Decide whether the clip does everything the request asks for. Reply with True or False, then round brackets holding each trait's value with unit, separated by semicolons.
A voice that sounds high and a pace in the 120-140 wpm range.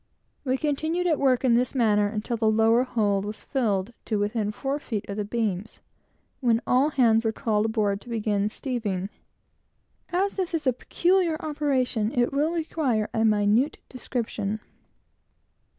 False (230 Hz; 155 wpm)